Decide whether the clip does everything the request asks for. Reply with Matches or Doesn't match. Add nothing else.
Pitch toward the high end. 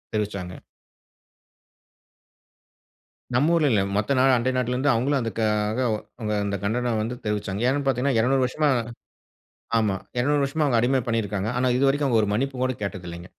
Doesn't match